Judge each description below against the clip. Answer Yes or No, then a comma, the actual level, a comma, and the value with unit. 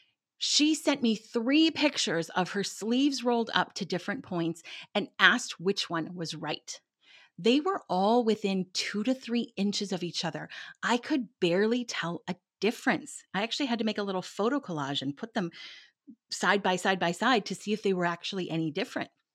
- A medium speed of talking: Yes, average, 190 wpm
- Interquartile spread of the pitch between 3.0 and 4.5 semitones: No, average, 4.9 semitones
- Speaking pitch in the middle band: No, high, 200 Hz